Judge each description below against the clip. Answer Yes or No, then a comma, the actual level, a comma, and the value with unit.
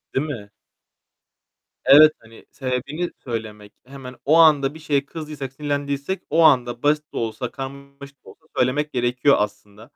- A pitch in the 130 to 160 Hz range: Yes, medium, 140 Hz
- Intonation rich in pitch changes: No, average, 3.3 semitones